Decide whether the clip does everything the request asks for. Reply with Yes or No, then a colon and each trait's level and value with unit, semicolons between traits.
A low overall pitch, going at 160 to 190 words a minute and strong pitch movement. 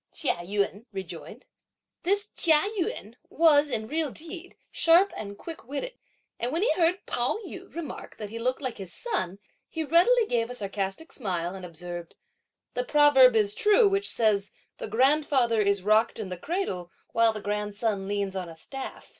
No: high, 235 Hz; average, 170 wpm; wide, 8.2 semitones